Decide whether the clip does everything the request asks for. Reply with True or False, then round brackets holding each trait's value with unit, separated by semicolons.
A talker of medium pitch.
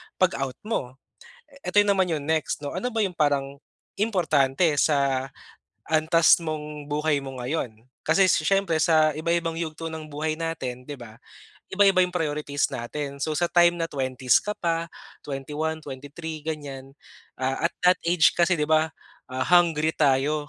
True (155 Hz)